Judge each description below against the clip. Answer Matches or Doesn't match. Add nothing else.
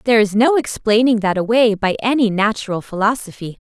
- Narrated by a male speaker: Doesn't match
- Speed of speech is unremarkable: Matches